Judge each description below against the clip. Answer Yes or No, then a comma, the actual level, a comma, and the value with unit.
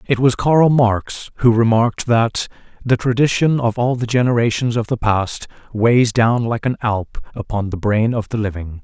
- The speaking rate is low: No, average, 185 wpm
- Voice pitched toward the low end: Yes, low, 115 Hz